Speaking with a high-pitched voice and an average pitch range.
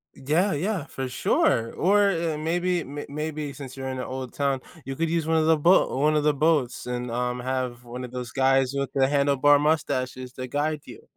No: medium, 140 Hz; average, 3.4 semitones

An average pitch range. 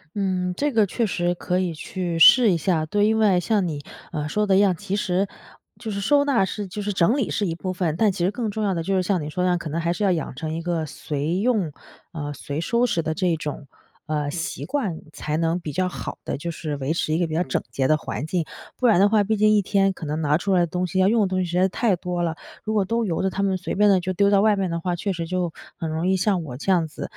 Yes: average, 3.6 semitones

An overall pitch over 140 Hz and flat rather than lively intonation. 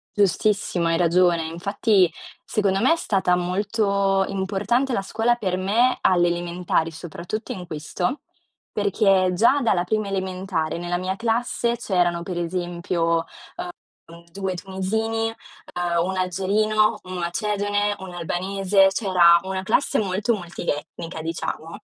No: high, 190 Hz; average, 3.0 semitones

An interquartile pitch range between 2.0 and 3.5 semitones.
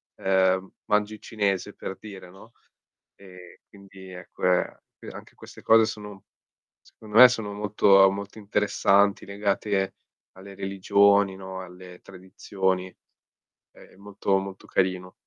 No: narrow, 1.4 semitones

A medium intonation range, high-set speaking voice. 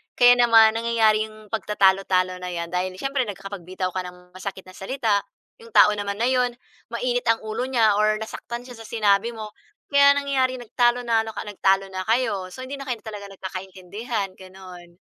Yes: average, 3.9 semitones; high, 215 Hz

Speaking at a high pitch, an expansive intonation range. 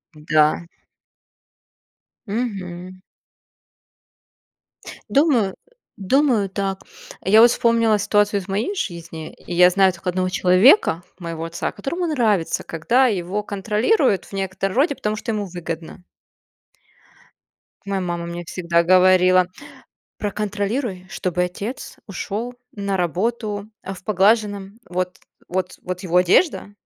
No: high, 195 Hz; average, 3.1 semitones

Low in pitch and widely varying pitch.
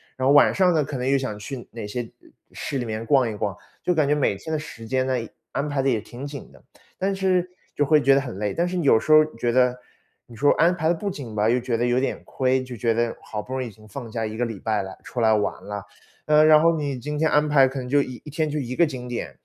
No: low, 130 Hz; average, 4.5 semitones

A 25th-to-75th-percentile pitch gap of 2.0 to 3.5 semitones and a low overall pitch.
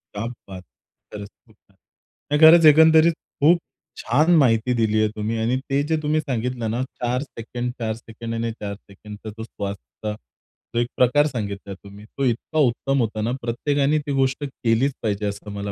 No: average, 4.4 semitones; low, 115 Hz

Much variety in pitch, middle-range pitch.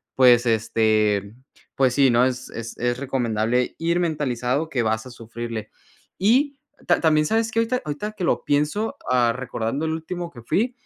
No: wide, 6.1 semitones; low, 130 Hz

